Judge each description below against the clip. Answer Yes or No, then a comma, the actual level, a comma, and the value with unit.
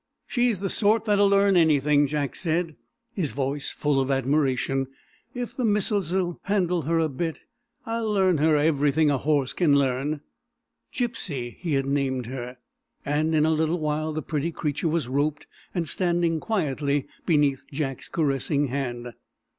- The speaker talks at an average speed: Yes, average, 155 wpm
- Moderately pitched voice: Yes, medium, 155 Hz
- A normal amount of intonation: Yes, average, 4.0 semitones